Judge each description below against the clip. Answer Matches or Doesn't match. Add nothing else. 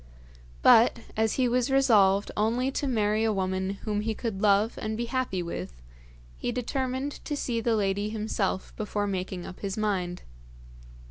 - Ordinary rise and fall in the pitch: Matches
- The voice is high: Matches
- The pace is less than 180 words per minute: Matches